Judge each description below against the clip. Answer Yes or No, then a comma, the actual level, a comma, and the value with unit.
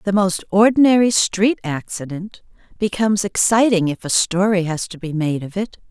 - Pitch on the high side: Yes, high, 195 Hz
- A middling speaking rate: Yes, average, 160 wpm